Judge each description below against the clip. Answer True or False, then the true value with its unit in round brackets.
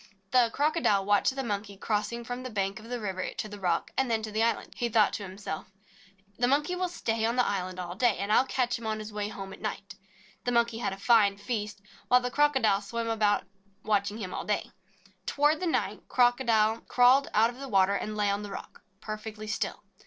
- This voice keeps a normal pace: False (225 wpm)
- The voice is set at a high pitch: True (220 Hz)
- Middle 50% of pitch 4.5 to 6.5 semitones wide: False (3.3 semitones)